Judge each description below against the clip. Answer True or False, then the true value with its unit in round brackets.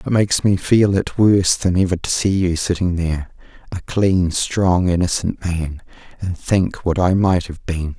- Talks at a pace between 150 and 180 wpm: False (190 wpm)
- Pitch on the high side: False (90 Hz)